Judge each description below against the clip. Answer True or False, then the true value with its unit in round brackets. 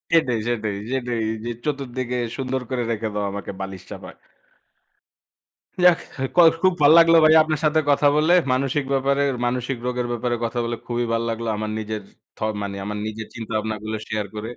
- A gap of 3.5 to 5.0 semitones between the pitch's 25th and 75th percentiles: True (4.0 semitones)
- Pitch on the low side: True (120 Hz)